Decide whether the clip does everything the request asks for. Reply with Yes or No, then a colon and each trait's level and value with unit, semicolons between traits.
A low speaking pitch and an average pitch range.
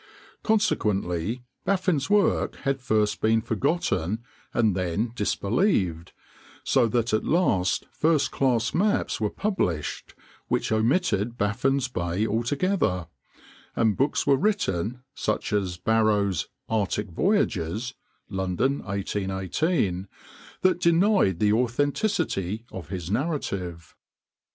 No: low, 110 Hz; wide, 6.9 semitones